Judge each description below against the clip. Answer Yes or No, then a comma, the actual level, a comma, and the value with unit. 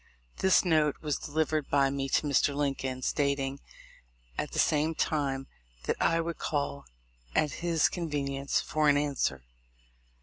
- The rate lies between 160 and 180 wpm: No, average, 140 wpm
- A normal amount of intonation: No, narrow, 2.1 semitones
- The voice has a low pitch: No, medium, 145 Hz